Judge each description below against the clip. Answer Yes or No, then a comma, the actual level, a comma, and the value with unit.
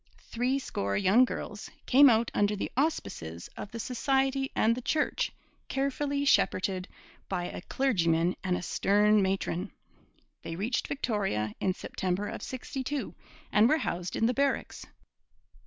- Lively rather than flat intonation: Yes, wide, 6.2 semitones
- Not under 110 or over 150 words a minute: Yes, average, 140 wpm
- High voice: Yes, high, 215 Hz